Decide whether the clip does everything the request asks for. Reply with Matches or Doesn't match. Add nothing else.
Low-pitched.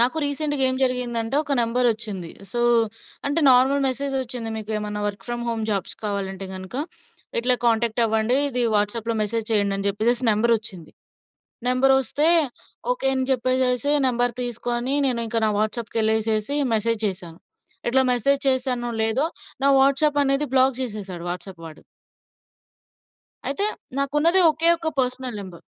Doesn't match